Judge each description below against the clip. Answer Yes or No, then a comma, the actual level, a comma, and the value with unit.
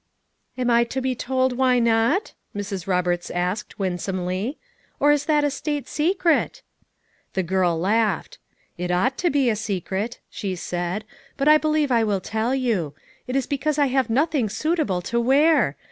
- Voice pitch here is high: Yes, high, 235 Hz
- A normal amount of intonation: No, wide, 6.9 semitones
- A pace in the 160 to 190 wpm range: Yes, average, 165 wpm